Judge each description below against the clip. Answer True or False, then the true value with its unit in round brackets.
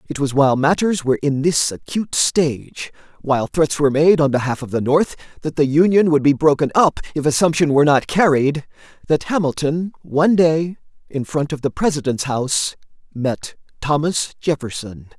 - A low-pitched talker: False (150 Hz)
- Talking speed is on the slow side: False (170 wpm)